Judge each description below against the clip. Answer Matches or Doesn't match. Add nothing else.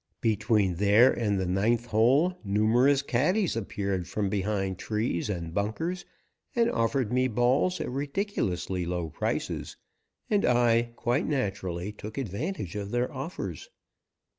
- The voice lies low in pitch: Matches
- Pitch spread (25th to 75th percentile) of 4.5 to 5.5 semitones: Matches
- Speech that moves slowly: Matches